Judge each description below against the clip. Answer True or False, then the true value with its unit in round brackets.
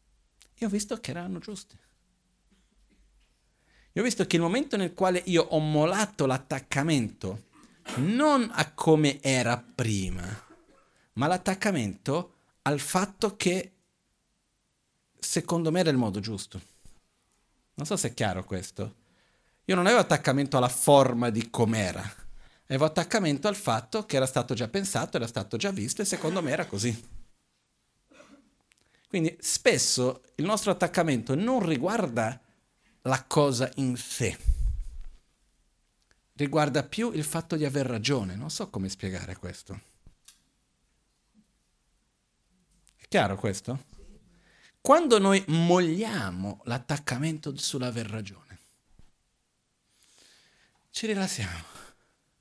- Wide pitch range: True (8.4 semitones)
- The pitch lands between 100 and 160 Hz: True (140 Hz)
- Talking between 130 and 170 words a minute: False (115 wpm)